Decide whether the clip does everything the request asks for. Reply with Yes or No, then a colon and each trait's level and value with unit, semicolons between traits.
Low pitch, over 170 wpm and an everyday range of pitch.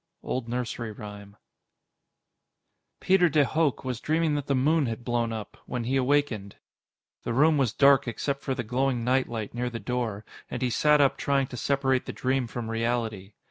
Yes: low, 125 Hz; average, 185 wpm; average, 3.2 semitones